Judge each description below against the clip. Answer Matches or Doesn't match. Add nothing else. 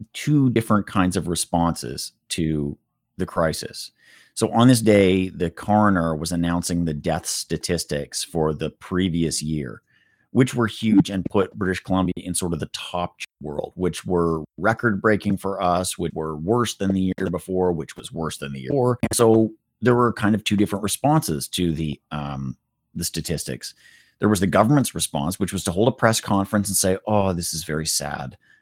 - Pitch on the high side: Doesn't match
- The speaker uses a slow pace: Doesn't match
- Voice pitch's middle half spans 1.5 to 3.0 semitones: Doesn't match